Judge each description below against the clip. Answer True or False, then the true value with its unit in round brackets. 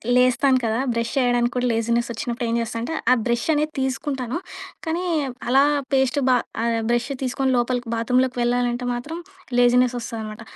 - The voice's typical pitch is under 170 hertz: False (245 Hz)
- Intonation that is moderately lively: False (1.8 semitones)